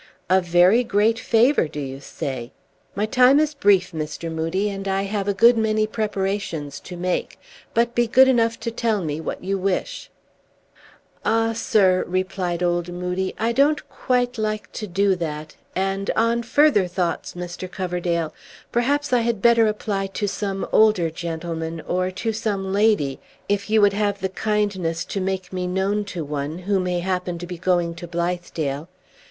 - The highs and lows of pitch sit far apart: No, average, 3.7 semitones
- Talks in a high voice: Yes, high, 195 Hz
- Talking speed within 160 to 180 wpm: Yes, average, 170 wpm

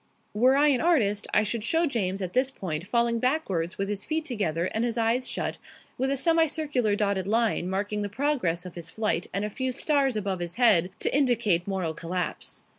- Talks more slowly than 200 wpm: No, fast, 205 wpm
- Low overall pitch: No, high, 215 Hz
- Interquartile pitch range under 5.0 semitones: No, wide, 5.6 semitones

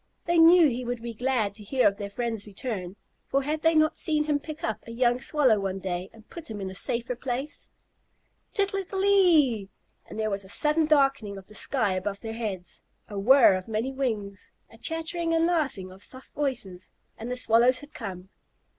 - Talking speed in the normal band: No, fast, 210 wpm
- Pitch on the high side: Yes, high, 240 Hz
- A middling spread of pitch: No, wide, 6.8 semitones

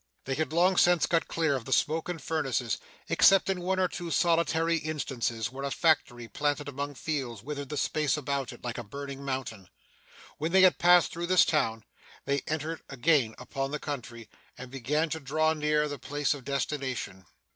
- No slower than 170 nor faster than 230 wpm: Yes, average, 190 wpm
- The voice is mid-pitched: Yes, medium, 145 Hz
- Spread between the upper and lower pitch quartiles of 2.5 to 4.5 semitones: Yes, average, 3.6 semitones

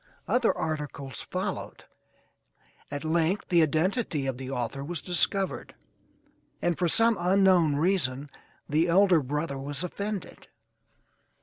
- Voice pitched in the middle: Yes, medium, 160 Hz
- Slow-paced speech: Yes, slow, 115 wpm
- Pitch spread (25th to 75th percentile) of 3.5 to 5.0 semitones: Yes, average, 4.5 semitones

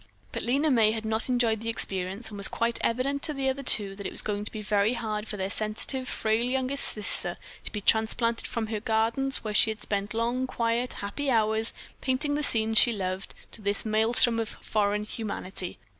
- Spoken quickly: Yes, fast, 210 wpm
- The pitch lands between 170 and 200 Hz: No, high, 220 Hz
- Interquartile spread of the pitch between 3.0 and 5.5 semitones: No, narrow, 2.6 semitones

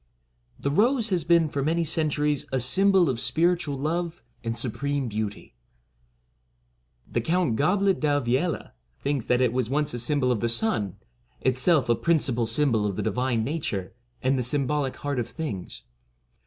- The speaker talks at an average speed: Yes, average, 170 wpm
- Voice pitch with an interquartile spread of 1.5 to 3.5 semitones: No, average, 5.2 semitones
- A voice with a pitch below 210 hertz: Yes, medium, 140 Hz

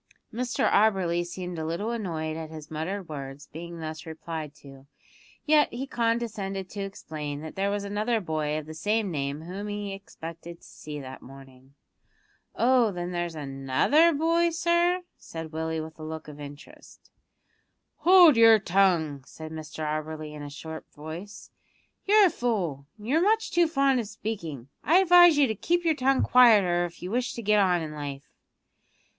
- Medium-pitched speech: Yes, medium, 175 Hz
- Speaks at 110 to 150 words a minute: No, average, 175 wpm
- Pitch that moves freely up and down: Yes, wide, 6.9 semitones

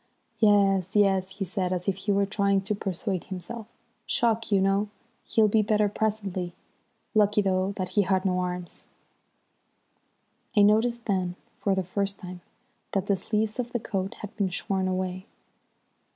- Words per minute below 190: Yes, average, 160 wpm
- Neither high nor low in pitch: No, high, 195 Hz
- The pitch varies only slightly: Yes, narrow, 2.1 semitones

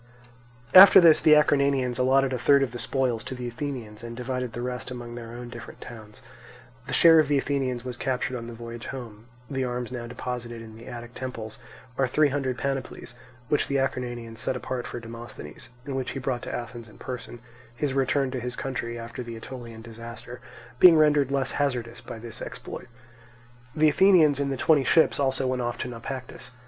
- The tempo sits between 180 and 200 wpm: Yes, average, 195 wpm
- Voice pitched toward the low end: Yes, low, 125 Hz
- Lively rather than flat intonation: No, narrow, 2.4 semitones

